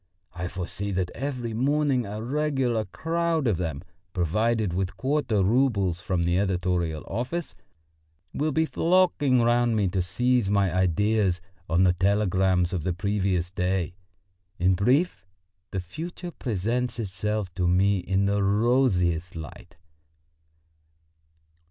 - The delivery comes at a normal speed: No, slow, 125 wpm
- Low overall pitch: Yes, low, 100 Hz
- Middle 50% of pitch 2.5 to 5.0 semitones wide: No, wide, 5.5 semitones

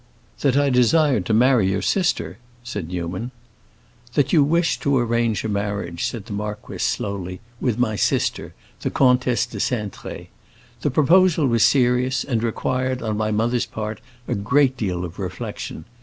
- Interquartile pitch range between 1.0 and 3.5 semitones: No, average, 4.1 semitones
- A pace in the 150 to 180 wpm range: Yes, average, 155 wpm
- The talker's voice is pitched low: Yes, low, 115 Hz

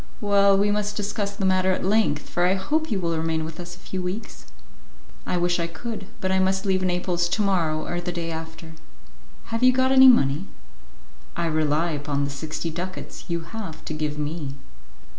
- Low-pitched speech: No, medium, 180 Hz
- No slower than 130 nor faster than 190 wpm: No, average, 200 wpm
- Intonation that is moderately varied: Yes, average, 3.7 semitones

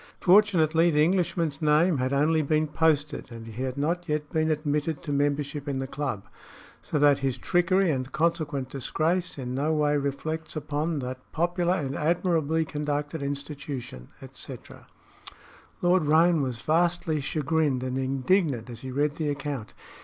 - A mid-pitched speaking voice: Yes, medium, 150 Hz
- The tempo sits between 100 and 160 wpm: Yes, average, 155 wpm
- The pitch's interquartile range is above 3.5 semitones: No, average, 2.8 semitones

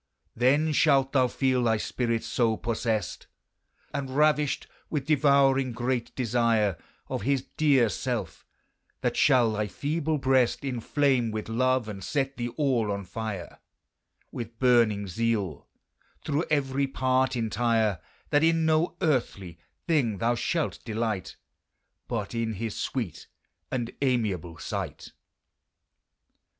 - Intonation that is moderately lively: Yes, average, 3.7 semitones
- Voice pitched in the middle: No, low, 120 Hz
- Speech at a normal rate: No, slow, 120 wpm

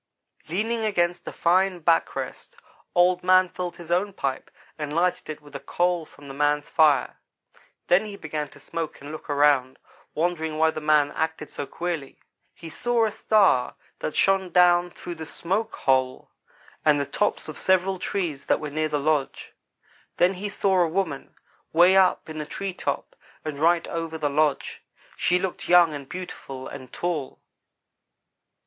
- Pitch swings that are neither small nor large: Yes, average, 3.5 semitones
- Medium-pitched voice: Yes, medium, 165 Hz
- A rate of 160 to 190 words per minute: Yes, average, 170 wpm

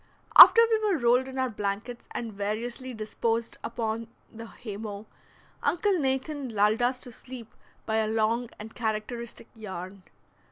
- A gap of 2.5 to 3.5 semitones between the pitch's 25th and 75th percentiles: Yes, average, 2.9 semitones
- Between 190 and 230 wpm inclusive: No, average, 145 wpm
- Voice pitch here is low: No, high, 230 Hz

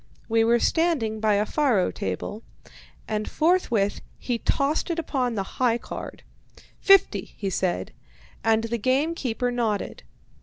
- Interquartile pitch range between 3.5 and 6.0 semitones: Yes, average, 4.5 semitones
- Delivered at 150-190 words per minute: No, average, 140 wpm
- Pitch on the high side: Yes, high, 230 Hz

